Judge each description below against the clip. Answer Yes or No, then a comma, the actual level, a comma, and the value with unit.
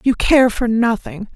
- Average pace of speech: Yes, average, 180 wpm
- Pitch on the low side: No, high, 230 Hz